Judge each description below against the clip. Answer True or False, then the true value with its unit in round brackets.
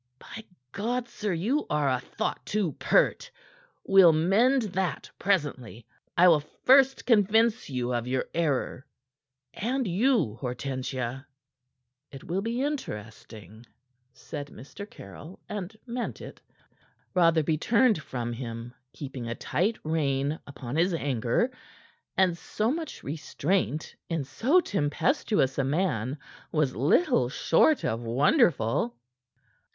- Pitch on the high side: False (160 Hz)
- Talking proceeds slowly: True (120 wpm)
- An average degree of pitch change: False (8.4 semitones)